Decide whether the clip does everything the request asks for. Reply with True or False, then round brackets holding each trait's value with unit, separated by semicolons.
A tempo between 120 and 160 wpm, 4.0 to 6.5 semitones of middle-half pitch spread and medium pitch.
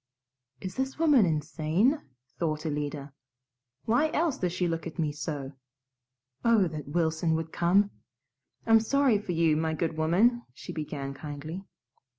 True (145 wpm; 5.6 semitones; 165 Hz)